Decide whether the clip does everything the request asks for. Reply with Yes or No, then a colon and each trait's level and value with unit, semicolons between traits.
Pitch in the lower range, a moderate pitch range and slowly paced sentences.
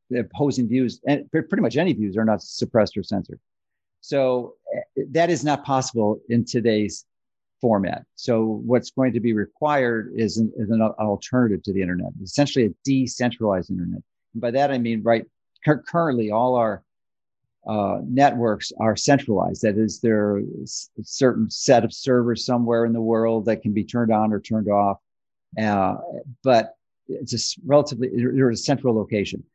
No: low, 115 Hz; average, 3.3 semitones; average, 165 wpm